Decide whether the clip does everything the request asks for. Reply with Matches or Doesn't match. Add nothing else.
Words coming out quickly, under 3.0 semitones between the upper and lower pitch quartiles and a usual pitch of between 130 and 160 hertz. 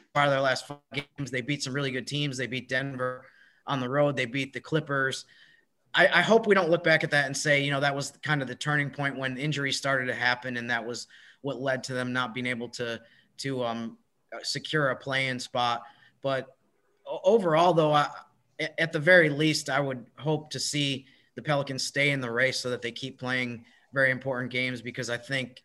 Matches